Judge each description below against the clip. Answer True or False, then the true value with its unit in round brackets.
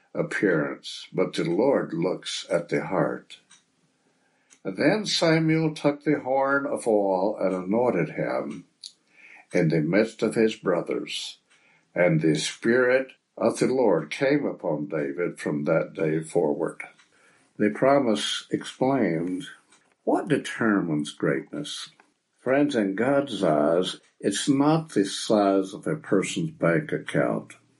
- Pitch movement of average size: False (7.4 semitones)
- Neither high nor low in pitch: False (115 Hz)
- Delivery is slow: True (125 wpm)